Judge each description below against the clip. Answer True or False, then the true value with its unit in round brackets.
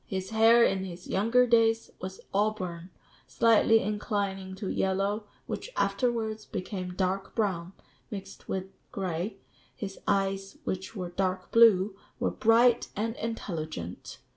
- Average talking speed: False (125 wpm)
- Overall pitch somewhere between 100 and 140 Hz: False (195 Hz)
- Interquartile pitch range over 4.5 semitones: False (3.0 semitones)